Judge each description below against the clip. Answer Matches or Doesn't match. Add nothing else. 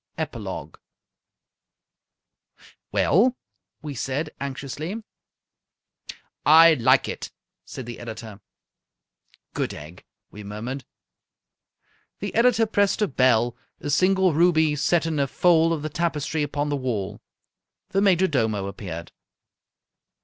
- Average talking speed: Doesn't match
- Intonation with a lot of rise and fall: Matches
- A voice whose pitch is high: Doesn't match